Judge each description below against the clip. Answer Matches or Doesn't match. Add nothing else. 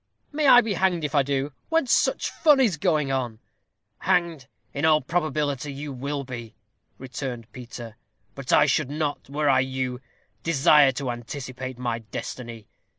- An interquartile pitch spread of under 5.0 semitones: Matches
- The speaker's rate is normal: Matches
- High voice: Doesn't match